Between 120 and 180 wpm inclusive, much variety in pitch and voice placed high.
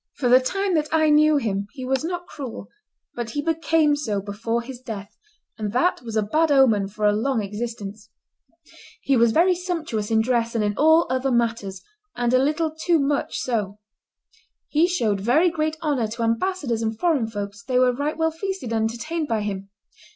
No: average, 190 wpm; wide, 5.9 semitones; very high, 250 Hz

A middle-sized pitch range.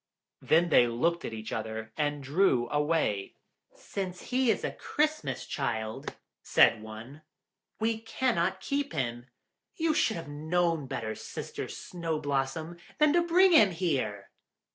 No: wide, 8.6 semitones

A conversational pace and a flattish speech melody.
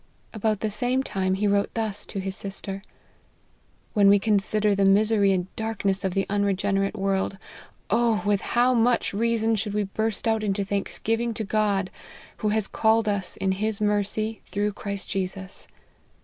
Yes: average, 170 wpm; narrow, 1.9 semitones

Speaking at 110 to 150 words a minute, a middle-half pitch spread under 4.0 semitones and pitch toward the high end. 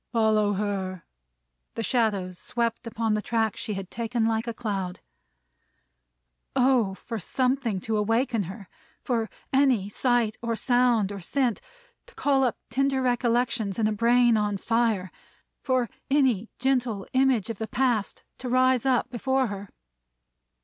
Yes: average, 140 wpm; average, 3.1 semitones; high, 230 Hz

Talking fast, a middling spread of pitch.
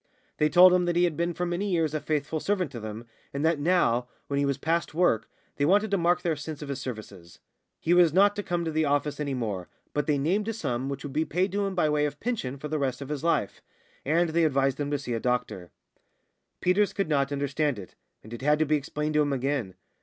Yes: fast, 250 wpm; average, 4.0 semitones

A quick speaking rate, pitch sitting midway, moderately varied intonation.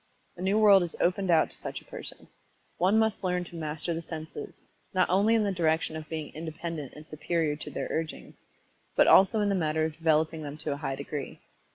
Yes: fast, 225 wpm; medium, 165 Hz; average, 3.0 semitones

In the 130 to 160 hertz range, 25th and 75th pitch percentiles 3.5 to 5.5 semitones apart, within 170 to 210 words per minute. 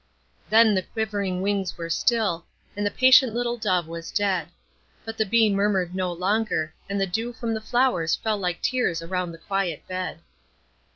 No: high, 200 Hz; average, 3.8 semitones; average, 175 wpm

